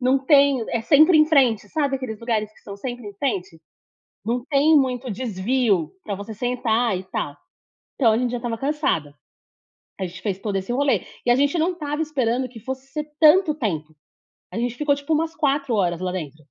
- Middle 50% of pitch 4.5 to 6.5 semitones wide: Yes, average, 5.3 semitones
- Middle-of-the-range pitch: No, high, 245 Hz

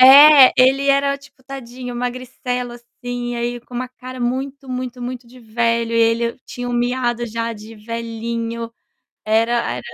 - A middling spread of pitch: No, narrow, 1.7 semitones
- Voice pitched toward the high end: Yes, high, 245 Hz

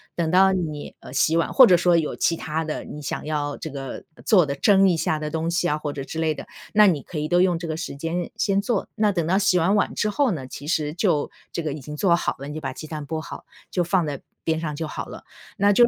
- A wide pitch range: No, average, 3.3 semitones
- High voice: No, medium, 165 Hz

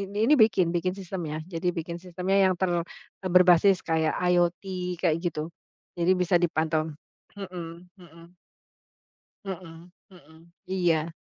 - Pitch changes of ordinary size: No, narrow, 1.9 semitones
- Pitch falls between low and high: Yes, medium, 175 Hz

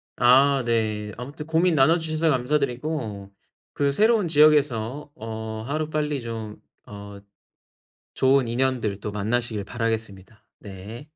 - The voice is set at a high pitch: No, low, 125 Hz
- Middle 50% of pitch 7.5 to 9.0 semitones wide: No, average, 5.3 semitones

